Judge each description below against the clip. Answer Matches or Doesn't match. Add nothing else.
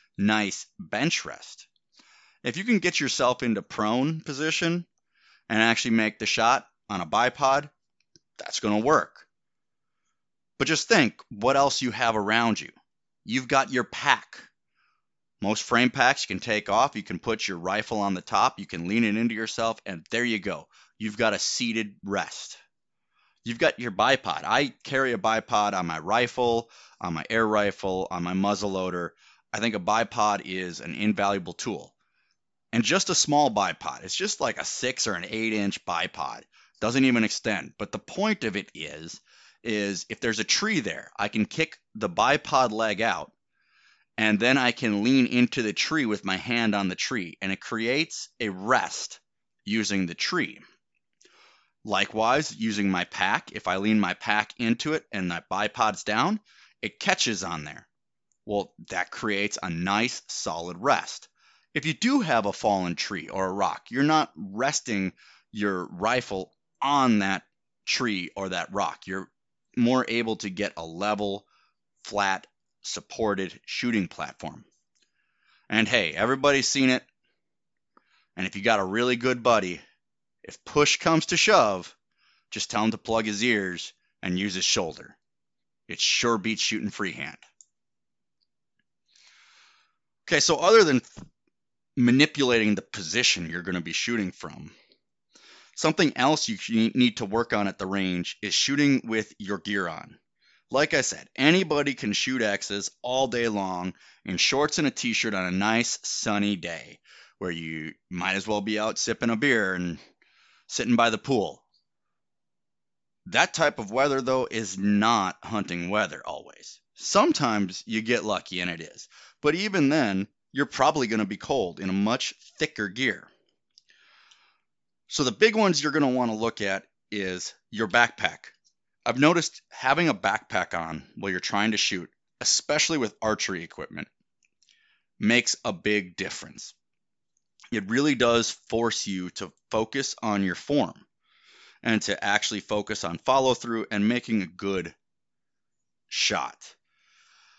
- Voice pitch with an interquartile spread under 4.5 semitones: Matches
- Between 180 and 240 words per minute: Doesn't match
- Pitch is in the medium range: Doesn't match